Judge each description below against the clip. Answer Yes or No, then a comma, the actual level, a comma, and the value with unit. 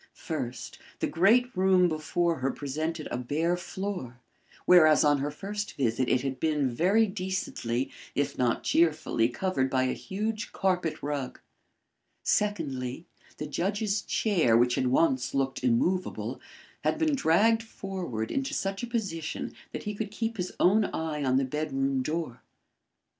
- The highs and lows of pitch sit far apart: Yes, wide, 6.5 semitones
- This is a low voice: No, medium, 160 Hz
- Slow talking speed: No, average, 145 wpm